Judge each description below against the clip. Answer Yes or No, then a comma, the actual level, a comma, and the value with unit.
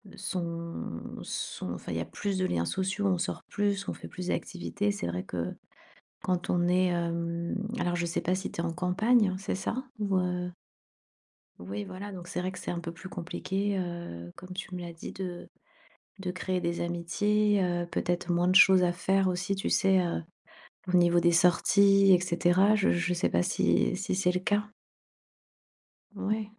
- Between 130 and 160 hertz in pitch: No, medium, 180 Hz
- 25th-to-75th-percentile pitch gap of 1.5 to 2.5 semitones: Yes, narrow, 2.0 semitones